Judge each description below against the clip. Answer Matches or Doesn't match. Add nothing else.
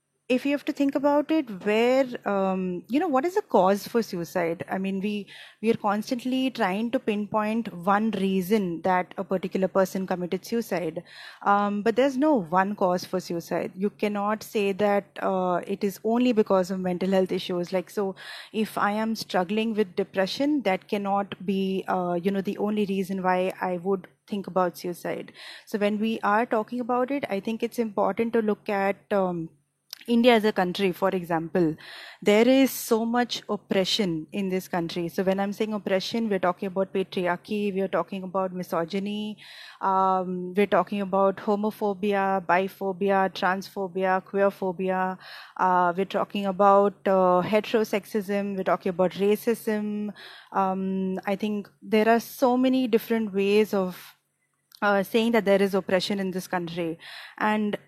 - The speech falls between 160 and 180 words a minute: Matches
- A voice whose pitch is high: Matches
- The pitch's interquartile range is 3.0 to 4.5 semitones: Doesn't match